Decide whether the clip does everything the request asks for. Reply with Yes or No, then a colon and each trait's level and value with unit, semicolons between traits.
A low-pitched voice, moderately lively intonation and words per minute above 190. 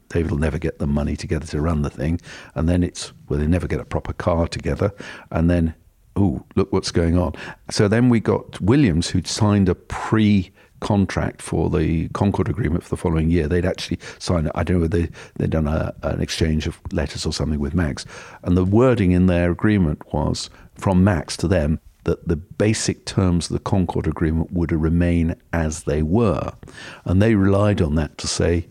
Yes: very low, 85 Hz; average, 3.3 semitones; average, 200 wpm